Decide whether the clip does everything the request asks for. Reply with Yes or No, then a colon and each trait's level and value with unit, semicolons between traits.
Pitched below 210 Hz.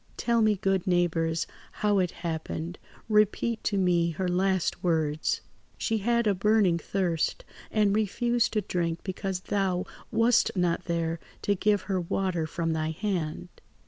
Yes: medium, 185 Hz